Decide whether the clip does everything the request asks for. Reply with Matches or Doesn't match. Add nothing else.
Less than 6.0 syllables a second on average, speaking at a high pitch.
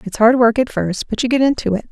Doesn't match